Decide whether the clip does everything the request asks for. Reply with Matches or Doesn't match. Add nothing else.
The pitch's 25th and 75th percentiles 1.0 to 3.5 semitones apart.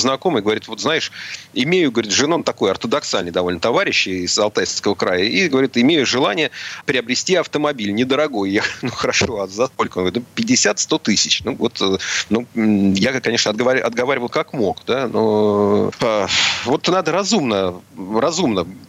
Doesn't match